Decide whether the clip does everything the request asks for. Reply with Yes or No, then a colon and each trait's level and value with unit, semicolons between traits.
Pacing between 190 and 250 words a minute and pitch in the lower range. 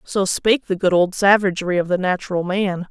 No: fast, 205 wpm; high, 190 Hz